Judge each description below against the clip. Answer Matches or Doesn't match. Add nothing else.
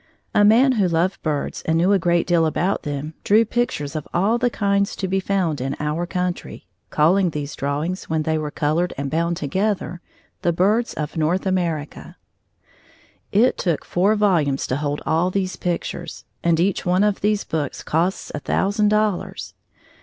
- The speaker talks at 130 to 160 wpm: Doesn't match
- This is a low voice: Doesn't match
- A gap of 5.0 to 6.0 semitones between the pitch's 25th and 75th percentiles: Doesn't match